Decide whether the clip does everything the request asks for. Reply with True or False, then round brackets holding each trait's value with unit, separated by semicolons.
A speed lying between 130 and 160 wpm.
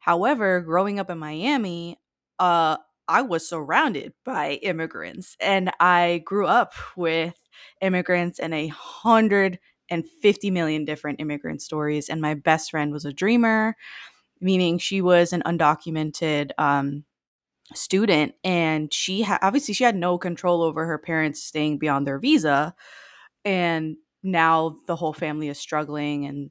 True (140 wpm)